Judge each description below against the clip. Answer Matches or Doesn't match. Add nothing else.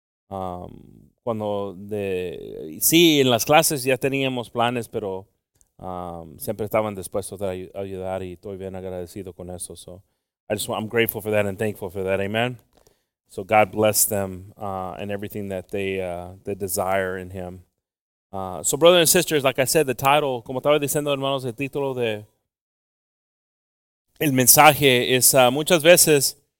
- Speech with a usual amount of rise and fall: Doesn't match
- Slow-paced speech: Doesn't match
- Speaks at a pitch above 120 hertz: Doesn't match